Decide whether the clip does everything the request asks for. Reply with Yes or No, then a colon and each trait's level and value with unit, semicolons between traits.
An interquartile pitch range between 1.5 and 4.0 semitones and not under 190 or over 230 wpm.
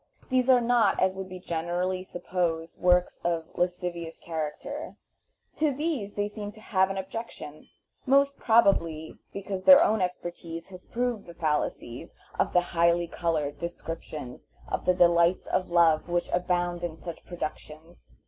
No: average, 3.1 semitones; average, 150 wpm